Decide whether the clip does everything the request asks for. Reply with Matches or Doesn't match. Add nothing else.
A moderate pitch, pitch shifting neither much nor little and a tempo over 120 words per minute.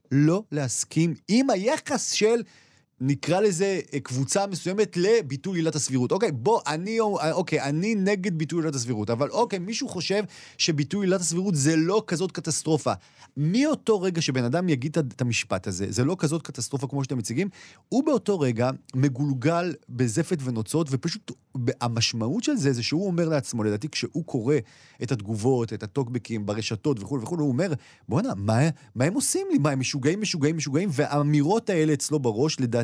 Doesn't match